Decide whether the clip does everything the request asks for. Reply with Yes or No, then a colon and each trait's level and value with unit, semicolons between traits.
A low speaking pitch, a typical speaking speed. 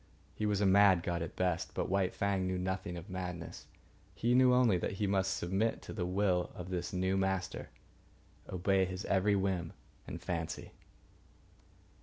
Yes: very low, 95 Hz; average, 170 wpm